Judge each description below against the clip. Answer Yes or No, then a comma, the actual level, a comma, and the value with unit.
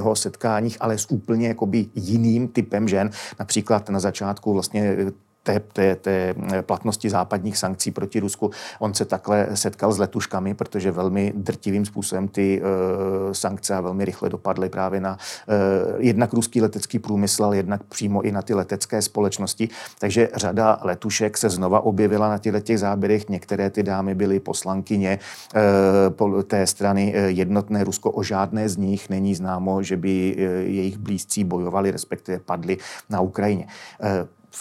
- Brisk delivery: No, average, 155 wpm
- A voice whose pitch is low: Yes, low, 100 Hz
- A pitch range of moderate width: No, narrow, 1.7 semitones